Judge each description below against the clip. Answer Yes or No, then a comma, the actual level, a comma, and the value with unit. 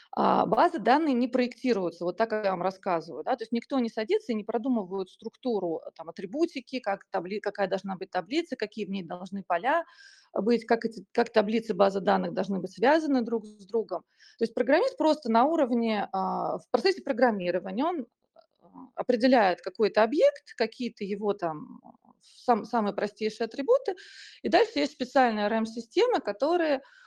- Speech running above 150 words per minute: Yes, fast, 160 wpm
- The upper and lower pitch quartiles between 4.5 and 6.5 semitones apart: Yes, average, 4.9 semitones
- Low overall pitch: No, high, 230 Hz